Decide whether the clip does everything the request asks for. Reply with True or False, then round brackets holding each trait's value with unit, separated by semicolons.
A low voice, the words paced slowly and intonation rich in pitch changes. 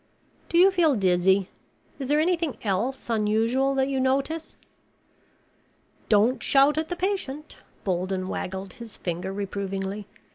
False (235 Hz; 130 wpm; 7.1 semitones)